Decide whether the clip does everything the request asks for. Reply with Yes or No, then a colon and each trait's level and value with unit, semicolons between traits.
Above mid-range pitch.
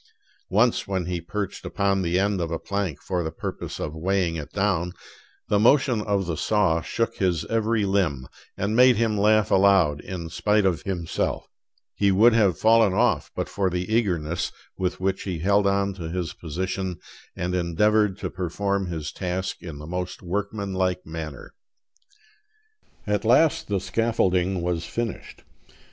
No: very low, 95 Hz